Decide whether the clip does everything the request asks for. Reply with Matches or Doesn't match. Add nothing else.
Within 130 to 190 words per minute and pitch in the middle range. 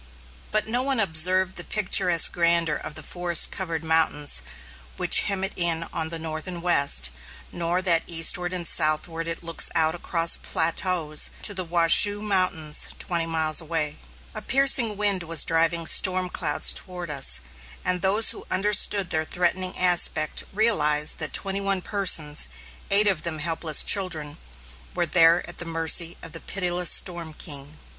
Matches